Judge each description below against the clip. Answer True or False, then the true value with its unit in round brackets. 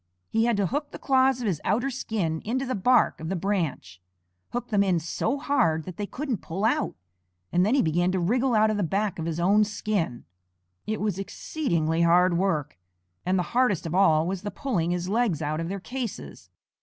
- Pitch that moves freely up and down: True (5.8 semitones)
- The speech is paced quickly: True (210 wpm)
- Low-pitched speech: False (195 Hz)